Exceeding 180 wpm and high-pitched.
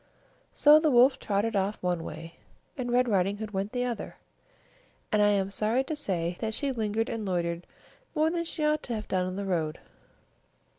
Yes: average, 195 wpm; high, 210 Hz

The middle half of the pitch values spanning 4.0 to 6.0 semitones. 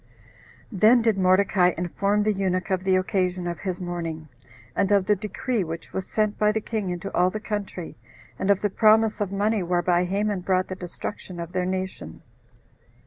No: narrow, 2.5 semitones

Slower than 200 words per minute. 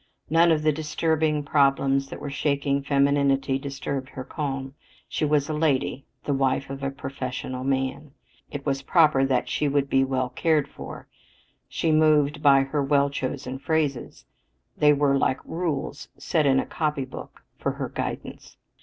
Yes: average, 160 wpm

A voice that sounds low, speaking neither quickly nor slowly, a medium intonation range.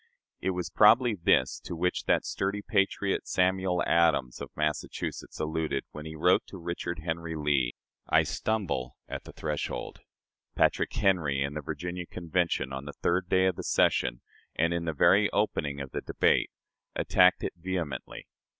Yes: very low, 85 Hz; average, 160 wpm; average, 3.6 semitones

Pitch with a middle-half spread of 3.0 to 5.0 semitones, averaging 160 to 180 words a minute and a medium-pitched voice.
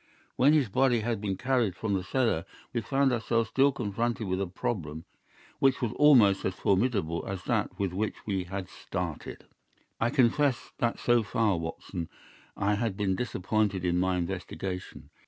No: average, 4.3 semitones; average, 165 wpm; low, 105 Hz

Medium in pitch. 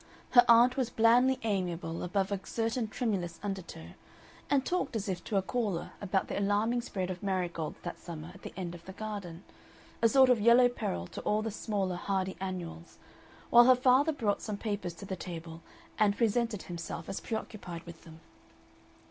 No: high, 200 Hz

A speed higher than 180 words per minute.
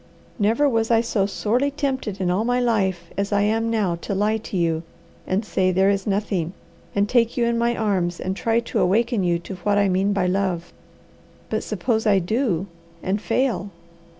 Yes: average, 195 wpm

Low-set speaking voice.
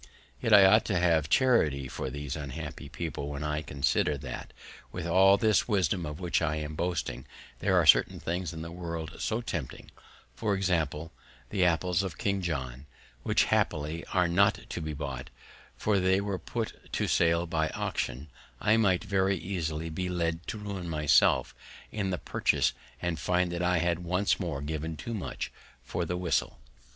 Yes: very low, 85 Hz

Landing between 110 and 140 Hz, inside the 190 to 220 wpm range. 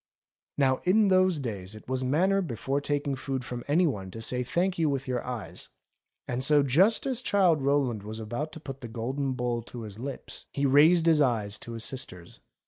Yes: low, 135 Hz; fast, 205 wpm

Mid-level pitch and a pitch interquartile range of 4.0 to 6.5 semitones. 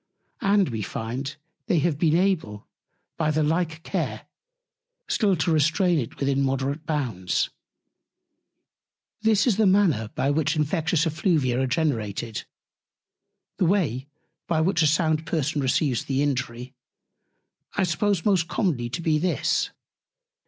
Yes: medium, 155 Hz; average, 4.7 semitones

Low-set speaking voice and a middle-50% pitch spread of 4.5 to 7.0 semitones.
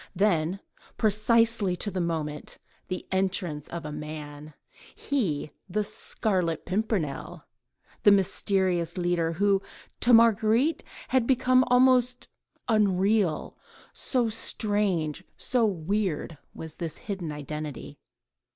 No: high, 190 Hz; average, 5.1 semitones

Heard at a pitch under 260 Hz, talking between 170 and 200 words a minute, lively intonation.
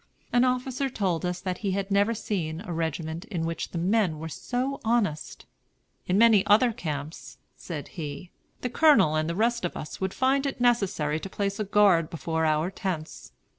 Yes: high, 190 Hz; average, 185 wpm; wide, 5.8 semitones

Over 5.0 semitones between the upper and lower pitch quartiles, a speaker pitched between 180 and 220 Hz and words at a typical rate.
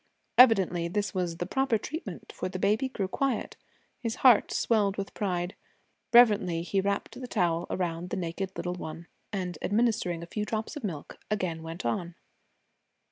No: average, 3.9 semitones; high, 190 Hz; average, 165 wpm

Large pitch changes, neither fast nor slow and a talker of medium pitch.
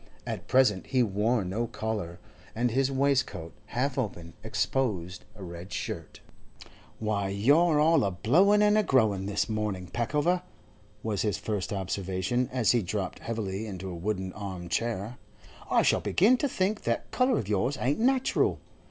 No: wide, 5.7 semitones; average, 160 wpm; low, 110 Hz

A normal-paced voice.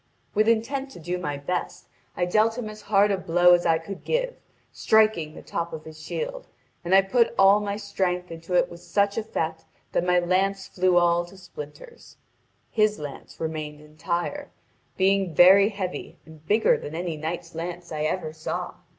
Yes: average, 180 wpm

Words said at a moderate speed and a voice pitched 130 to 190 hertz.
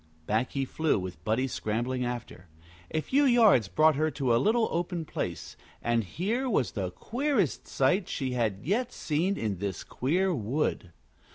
Yes: average, 165 wpm; low, 135 Hz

